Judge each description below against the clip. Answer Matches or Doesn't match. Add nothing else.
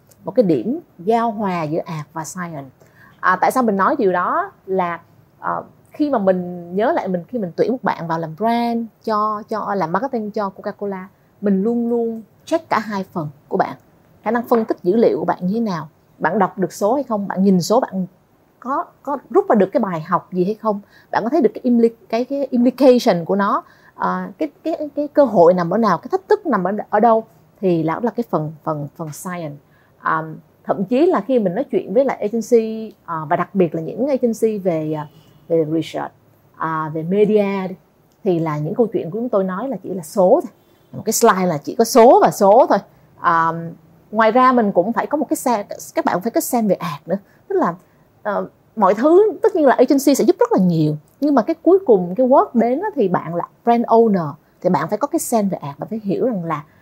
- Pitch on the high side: Matches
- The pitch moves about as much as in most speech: Doesn't match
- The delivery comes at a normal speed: Matches